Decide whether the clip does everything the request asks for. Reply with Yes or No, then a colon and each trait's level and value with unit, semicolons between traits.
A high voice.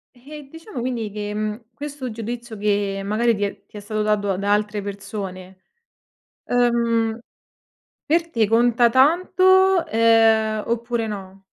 Yes: high, 225 Hz